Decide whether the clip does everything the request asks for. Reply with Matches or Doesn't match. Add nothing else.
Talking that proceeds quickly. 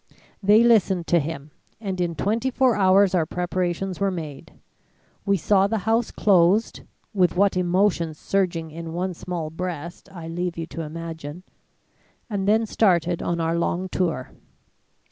Doesn't match